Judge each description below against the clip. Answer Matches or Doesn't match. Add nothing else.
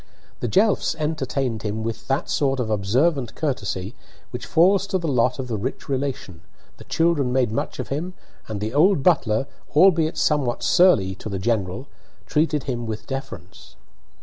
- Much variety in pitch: Matches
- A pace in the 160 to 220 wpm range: Matches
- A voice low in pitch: Matches